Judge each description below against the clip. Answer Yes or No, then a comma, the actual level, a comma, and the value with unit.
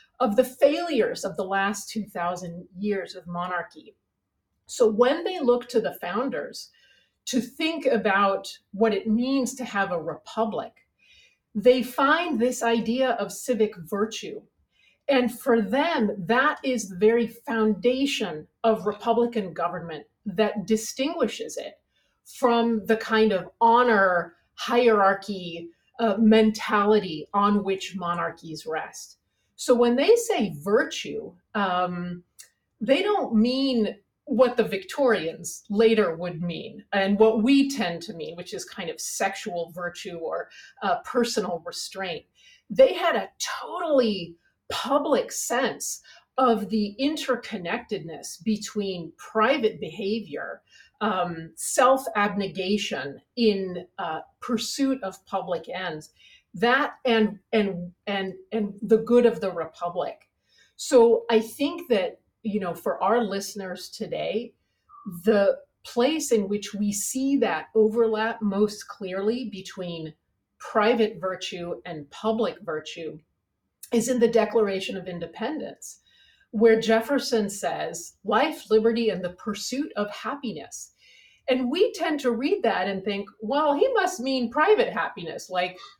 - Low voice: No, high, 220 Hz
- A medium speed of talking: No, slow, 125 wpm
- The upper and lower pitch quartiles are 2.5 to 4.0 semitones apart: No, average, 4.5 semitones